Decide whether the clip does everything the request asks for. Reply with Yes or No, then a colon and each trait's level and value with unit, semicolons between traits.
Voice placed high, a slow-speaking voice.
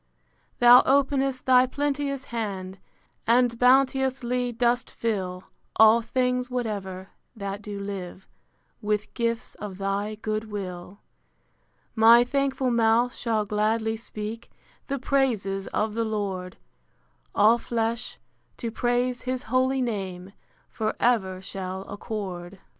Yes: high, 225 Hz; slow, 115 wpm